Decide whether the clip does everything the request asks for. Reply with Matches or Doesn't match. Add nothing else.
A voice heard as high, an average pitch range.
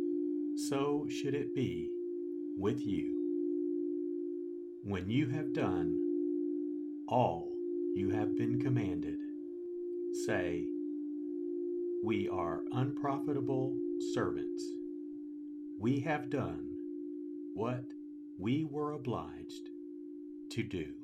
Doesn't match